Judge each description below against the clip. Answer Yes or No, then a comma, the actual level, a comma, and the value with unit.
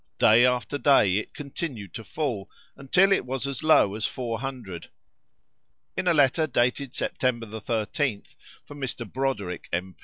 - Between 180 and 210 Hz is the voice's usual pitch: No, low, 125 Hz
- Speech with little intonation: No, average, 4.4 semitones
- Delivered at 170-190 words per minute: No, average, 150 wpm